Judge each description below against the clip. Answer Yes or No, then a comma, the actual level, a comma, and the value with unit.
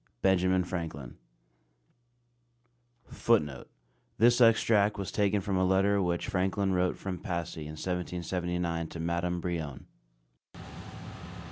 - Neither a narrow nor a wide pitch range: No, narrow, 2.3 semitones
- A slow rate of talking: Yes, slow, 105 wpm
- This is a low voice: Yes, very low, 90 Hz